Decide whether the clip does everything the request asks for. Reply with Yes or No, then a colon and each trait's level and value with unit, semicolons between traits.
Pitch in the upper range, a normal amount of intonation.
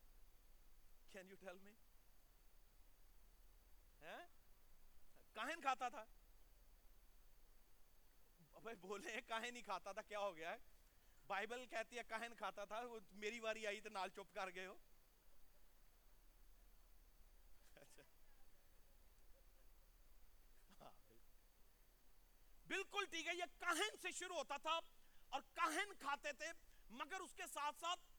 No: high, 235 Hz; wide, 8.5 semitones